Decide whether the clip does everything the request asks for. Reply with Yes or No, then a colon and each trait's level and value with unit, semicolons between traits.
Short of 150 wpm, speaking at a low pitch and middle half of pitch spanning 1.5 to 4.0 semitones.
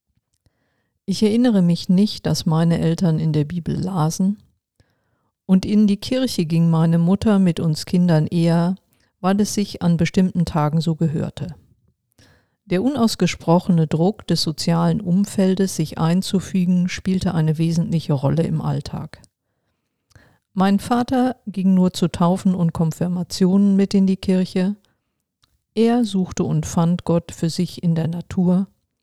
No: average, 135 wpm; medium, 180 Hz; narrow, 2.5 semitones